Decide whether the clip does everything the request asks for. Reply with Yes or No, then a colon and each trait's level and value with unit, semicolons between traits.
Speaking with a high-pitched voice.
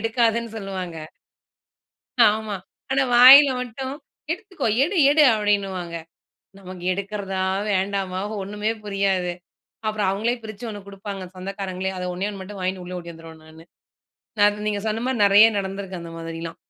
Yes: high, 200 Hz